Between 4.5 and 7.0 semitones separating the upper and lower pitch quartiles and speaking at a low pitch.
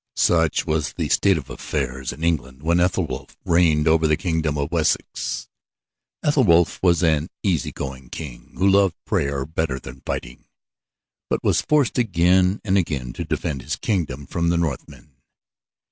No: average, 4.0 semitones; very low, 80 Hz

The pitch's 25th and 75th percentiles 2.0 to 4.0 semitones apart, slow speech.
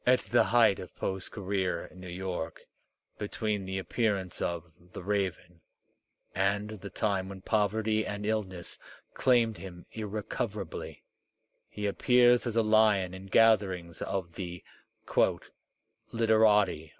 Yes: average, 2.8 semitones; slow, 125 wpm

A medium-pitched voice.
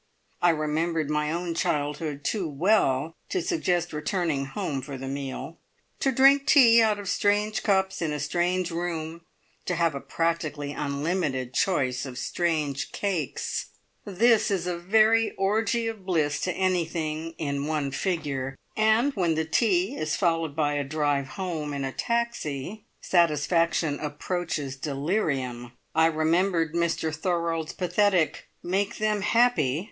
Yes: medium, 165 Hz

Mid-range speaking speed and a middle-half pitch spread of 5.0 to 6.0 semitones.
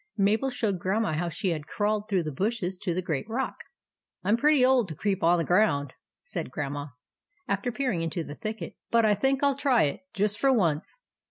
No: fast, 225 wpm; wide, 5.6 semitones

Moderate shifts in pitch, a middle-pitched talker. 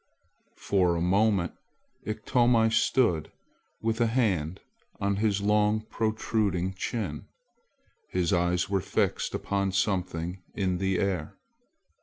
No: average, 3.3 semitones; low, 100 Hz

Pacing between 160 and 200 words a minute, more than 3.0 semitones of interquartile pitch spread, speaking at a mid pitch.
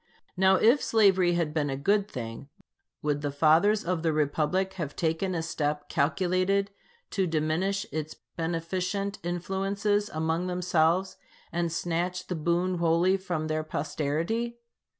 No: slow, 135 wpm; average, 3.4 semitones; medium, 175 Hz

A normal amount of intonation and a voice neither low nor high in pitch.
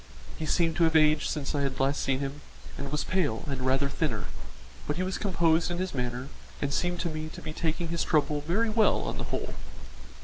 Yes: average, 3.4 semitones; medium, 155 Hz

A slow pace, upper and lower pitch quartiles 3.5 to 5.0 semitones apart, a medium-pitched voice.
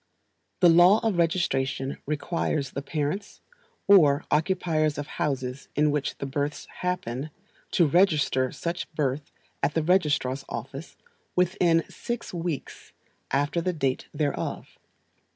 Yes: slow, 120 wpm; average, 3.8 semitones; medium, 150 Hz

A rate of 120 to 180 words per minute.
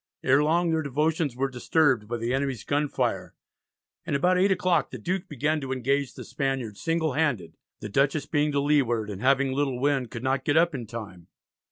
No: average, 195 wpm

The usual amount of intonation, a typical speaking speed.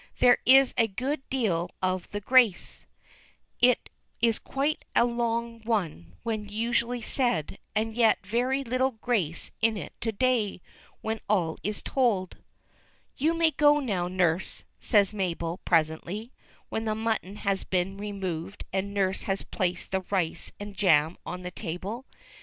Yes: average, 4.4 semitones; average, 150 wpm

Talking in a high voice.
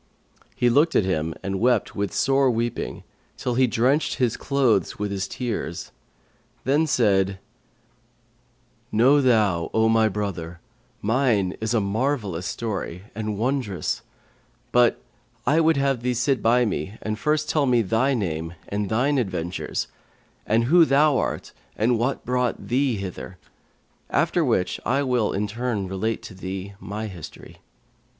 No: low, 115 Hz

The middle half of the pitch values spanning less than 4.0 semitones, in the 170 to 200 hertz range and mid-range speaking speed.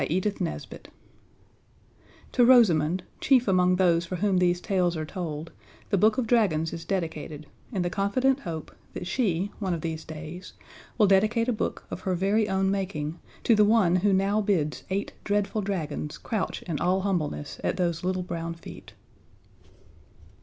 Yes: average, 3.5 semitones; medium, 185 Hz; average, 165 wpm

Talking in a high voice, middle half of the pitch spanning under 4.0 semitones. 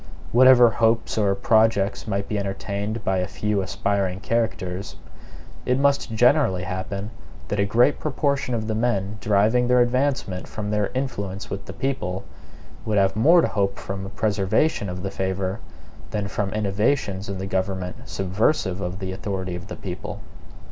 No: low, 100 Hz; average, 3.2 semitones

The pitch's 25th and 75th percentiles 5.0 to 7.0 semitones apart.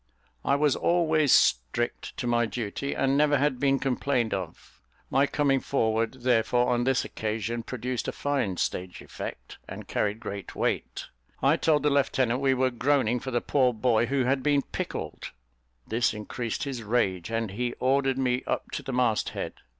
No: average, 3.3 semitones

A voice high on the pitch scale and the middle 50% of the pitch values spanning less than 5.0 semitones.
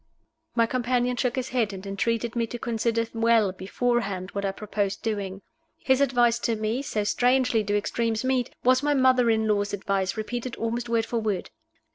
Yes: high, 230 Hz; average, 2.9 semitones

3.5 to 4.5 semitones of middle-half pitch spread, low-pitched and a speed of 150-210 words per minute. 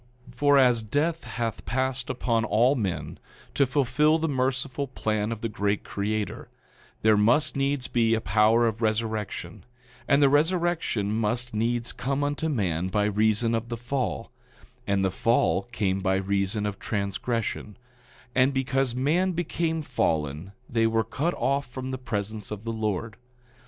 Yes: average, 4.2 semitones; low, 115 Hz; average, 155 wpm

